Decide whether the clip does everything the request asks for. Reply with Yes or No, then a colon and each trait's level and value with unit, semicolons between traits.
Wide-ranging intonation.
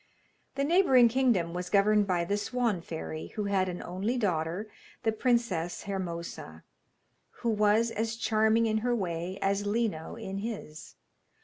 No: average, 4.4 semitones